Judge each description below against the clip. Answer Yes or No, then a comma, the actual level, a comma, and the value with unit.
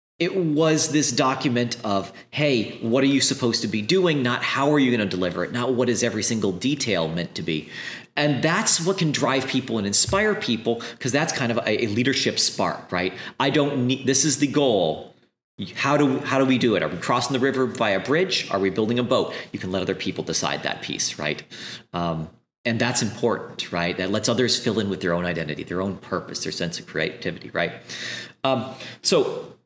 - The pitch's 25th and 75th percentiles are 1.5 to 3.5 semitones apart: No, average, 4.0 semitones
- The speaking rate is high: Yes, fast, 220 wpm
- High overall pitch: No, low, 125 Hz